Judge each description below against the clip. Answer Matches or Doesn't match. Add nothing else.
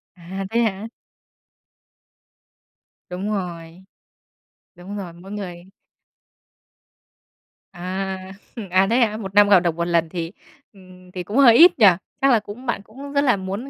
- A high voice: Matches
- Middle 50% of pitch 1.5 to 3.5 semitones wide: Matches